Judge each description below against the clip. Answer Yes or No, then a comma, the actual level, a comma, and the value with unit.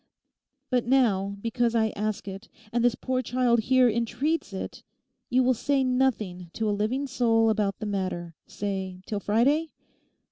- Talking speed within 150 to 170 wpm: Yes, average, 155 wpm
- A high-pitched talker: Yes, high, 230 Hz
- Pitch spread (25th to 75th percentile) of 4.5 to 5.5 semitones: No, average, 3.8 semitones